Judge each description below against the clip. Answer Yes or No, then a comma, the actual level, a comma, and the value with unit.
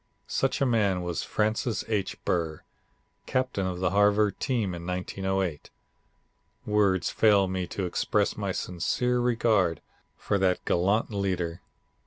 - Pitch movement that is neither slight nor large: Yes, average, 3.0 semitones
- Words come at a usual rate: No, slow, 130 wpm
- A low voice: Yes, very low, 95 Hz